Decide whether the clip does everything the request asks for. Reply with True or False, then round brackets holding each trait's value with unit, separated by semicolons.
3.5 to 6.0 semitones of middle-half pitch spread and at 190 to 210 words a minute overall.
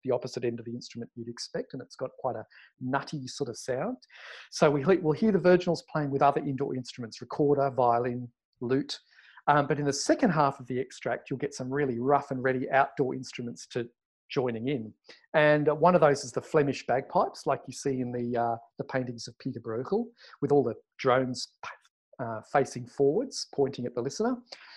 False (2.9 semitones; 200 wpm)